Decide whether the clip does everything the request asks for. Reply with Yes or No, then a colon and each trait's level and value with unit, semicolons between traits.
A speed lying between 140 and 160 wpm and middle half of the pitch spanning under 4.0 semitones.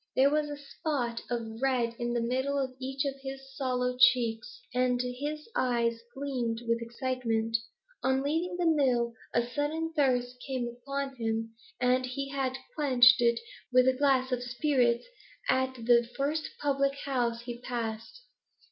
Yes: average, 155 wpm; narrow, 2.5 semitones